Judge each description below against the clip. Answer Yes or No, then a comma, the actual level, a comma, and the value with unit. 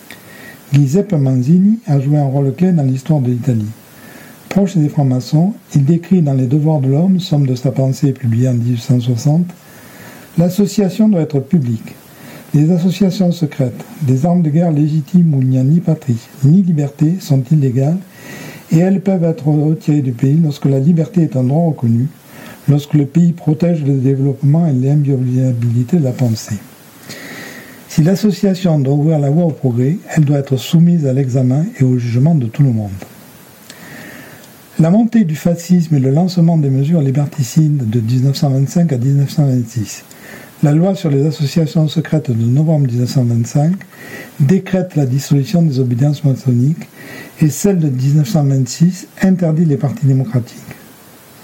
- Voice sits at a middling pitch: Yes, medium, 150 Hz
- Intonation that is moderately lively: Yes, average, 4.2 semitones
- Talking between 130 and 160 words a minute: Yes, average, 155 wpm